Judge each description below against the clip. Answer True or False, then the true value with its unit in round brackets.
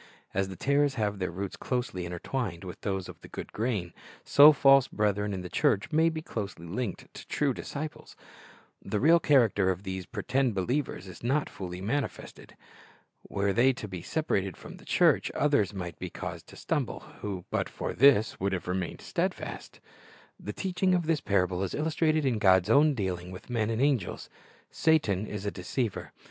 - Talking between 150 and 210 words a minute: True (180 wpm)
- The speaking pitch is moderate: False (105 Hz)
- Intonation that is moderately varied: False (6.8 semitones)